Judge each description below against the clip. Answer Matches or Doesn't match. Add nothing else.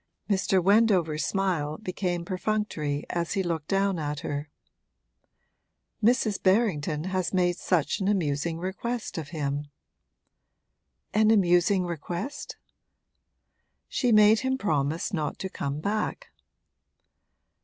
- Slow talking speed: Matches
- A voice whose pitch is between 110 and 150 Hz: Doesn't match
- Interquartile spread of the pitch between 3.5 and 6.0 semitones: Matches